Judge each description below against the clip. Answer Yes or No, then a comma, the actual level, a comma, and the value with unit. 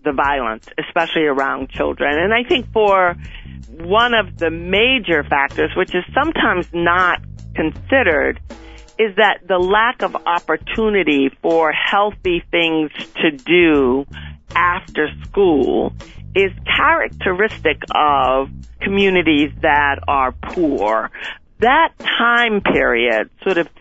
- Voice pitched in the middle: Yes, medium, 175 Hz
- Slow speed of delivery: Yes, slow, 110 wpm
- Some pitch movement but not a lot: No, wide, 6.7 semitones